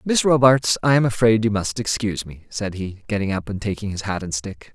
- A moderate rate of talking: No, fast, 240 wpm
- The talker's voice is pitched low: Yes, low, 105 Hz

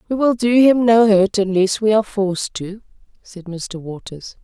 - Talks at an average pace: Yes, average, 190 wpm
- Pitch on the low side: No, high, 205 Hz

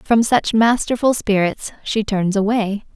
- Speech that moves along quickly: No, average, 140 wpm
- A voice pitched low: No, high, 215 Hz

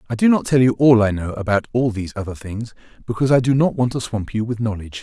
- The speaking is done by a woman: No, male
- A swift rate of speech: Yes, fast, 275 wpm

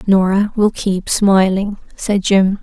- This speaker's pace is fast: No, slow, 135 wpm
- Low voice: No, high, 195 Hz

